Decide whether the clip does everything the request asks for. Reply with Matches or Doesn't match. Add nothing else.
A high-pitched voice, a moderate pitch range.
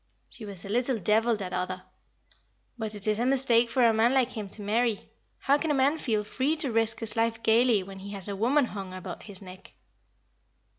Matches